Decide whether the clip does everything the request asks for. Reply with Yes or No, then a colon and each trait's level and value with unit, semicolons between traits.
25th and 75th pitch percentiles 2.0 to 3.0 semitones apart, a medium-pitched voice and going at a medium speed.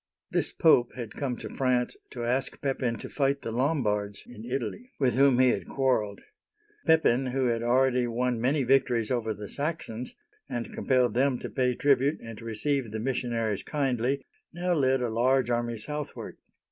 No: narrow, 2.5 semitones; low, 125 Hz; average, 175 wpm